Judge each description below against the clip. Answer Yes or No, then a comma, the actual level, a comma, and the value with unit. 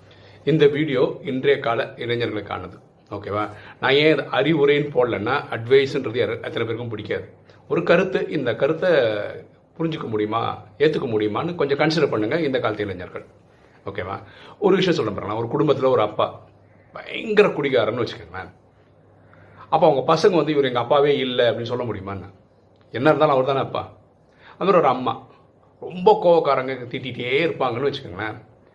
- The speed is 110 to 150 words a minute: Yes, fast, 130 wpm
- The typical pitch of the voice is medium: No, low, 125 Hz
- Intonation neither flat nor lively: No, wide, 6.3 semitones